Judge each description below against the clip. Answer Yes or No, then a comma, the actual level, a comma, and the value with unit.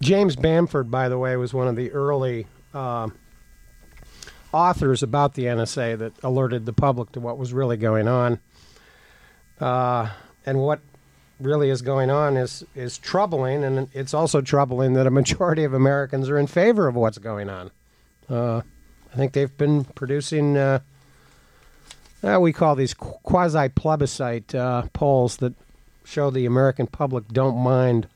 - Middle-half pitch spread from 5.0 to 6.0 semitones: No, average, 2.7 semitones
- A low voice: Yes, low, 130 Hz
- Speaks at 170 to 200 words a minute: No, average, 155 wpm